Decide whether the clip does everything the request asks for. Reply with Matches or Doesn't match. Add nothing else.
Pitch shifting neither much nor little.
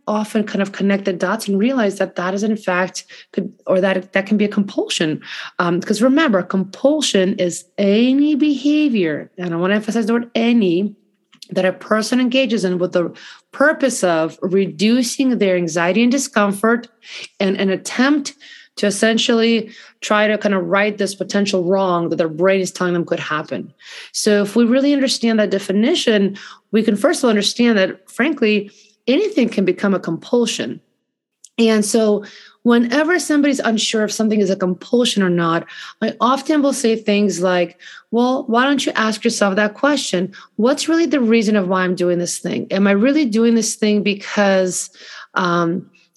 Matches